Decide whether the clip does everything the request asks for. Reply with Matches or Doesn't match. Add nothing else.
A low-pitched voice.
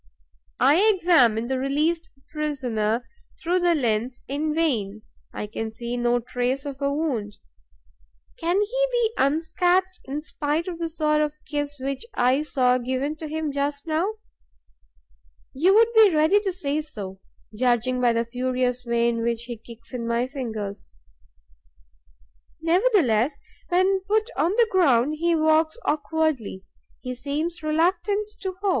Doesn't match